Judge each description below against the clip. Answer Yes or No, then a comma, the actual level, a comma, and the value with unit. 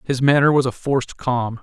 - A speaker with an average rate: No, fast, 220 wpm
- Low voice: Yes, low, 130 Hz